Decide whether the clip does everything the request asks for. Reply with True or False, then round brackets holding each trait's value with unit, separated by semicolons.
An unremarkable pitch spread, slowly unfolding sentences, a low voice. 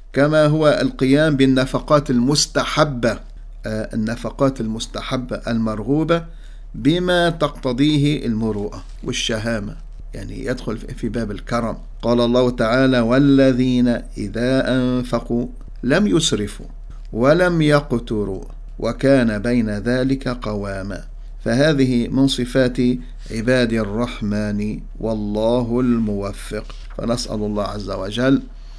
True (3.4 semitones; 90 wpm; 125 Hz)